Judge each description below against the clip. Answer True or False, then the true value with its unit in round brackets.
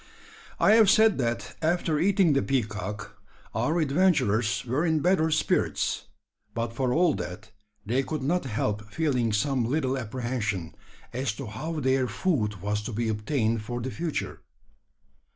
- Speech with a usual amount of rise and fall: False (6.3 semitones)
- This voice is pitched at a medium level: False (130 Hz)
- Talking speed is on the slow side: False (150 wpm)